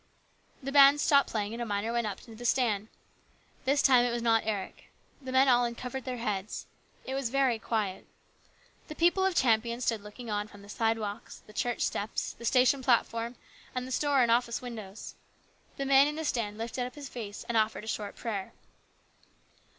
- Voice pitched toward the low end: No, high, 235 Hz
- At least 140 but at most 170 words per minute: No, average, 195 wpm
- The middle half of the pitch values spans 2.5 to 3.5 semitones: Yes, average, 3.2 semitones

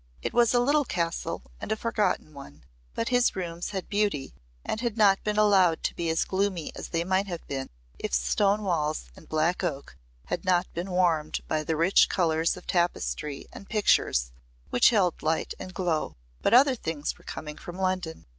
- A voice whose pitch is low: No, medium, 175 Hz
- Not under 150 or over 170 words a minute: No, average, 190 wpm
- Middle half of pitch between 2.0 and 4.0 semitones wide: No, average, 4.4 semitones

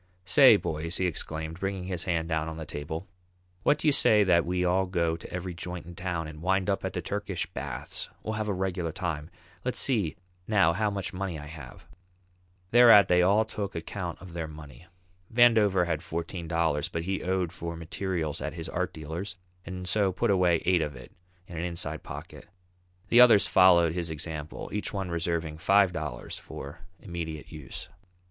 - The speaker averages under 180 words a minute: No, average, 190 wpm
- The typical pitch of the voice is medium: No, very low, 90 Hz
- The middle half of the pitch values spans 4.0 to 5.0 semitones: No, average, 3.0 semitones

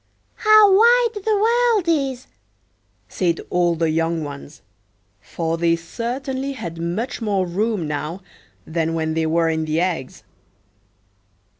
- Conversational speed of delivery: No, slow, 130 wpm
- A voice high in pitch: No, medium, 175 Hz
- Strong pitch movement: Yes, wide, 9.0 semitones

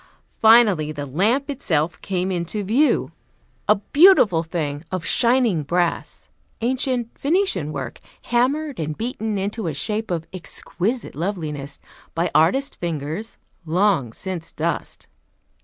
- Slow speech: Yes, slow, 120 wpm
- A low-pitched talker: No, medium, 185 Hz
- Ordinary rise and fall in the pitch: No, wide, 6.7 semitones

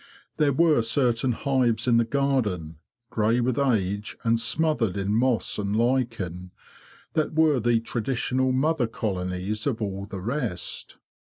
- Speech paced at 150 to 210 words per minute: No, average, 140 wpm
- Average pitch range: Yes, average, 4.2 semitones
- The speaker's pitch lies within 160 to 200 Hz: No, low, 115 Hz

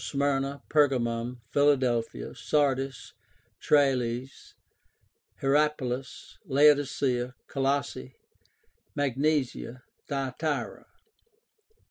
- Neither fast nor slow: No, slow, 50 wpm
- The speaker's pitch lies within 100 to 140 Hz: Yes, low, 135 Hz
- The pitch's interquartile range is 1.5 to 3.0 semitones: Yes, narrow, 2.4 semitones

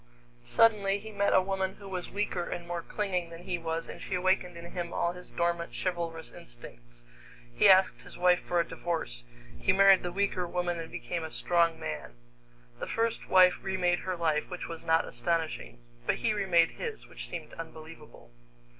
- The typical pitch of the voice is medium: Yes, medium, 175 Hz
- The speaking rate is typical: Yes, average, 185 wpm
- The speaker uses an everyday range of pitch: No, narrow, 2.3 semitones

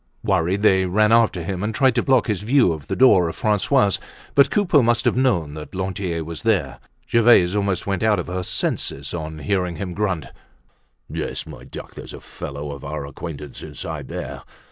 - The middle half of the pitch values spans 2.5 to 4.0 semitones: No, average, 4.7 semitones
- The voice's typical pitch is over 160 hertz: No, very low, 95 Hz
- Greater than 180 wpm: Yes, average, 195 wpm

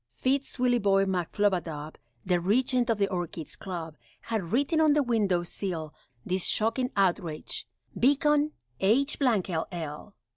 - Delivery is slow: Yes, slow, 120 wpm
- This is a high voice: Yes, high, 200 Hz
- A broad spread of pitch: Yes, wide, 6.3 semitones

